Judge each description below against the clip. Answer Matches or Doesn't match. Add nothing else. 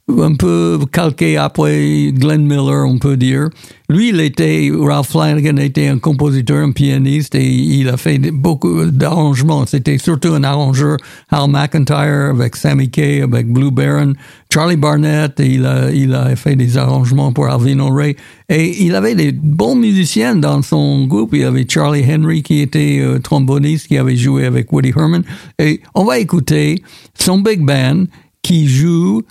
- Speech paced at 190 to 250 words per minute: Doesn't match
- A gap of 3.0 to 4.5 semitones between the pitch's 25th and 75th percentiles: Doesn't match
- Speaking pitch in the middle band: Matches